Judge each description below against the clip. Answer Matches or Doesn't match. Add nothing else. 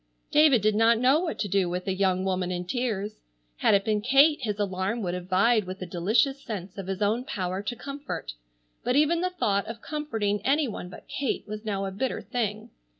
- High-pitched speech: Matches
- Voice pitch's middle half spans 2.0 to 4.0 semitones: Doesn't match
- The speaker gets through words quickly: Matches